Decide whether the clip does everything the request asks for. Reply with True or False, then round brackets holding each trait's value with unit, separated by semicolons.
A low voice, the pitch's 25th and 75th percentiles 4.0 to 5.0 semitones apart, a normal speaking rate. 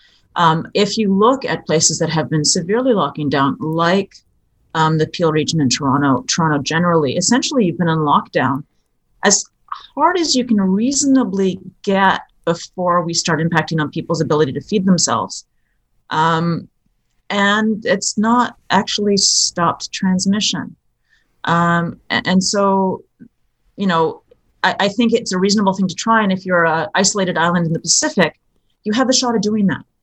False (185 Hz; 4.5 semitones; 160 wpm)